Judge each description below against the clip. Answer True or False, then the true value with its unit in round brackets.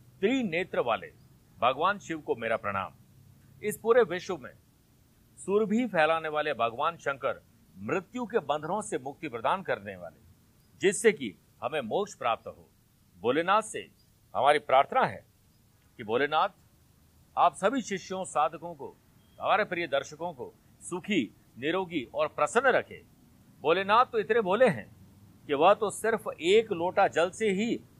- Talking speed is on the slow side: False (140 wpm)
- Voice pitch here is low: False (175 Hz)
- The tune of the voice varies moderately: False (6.6 semitones)